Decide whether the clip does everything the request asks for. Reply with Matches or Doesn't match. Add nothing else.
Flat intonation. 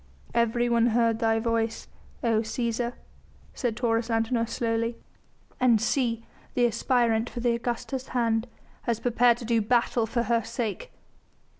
Matches